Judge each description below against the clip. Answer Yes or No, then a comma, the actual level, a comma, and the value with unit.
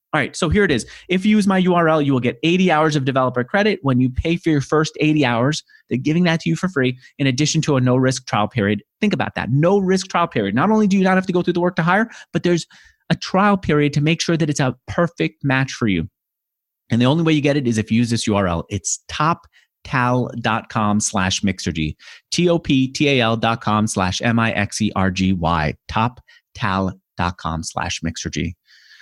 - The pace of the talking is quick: Yes, fast, 235 wpm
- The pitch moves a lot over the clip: Yes, wide, 7.9 semitones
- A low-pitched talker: Yes, low, 130 Hz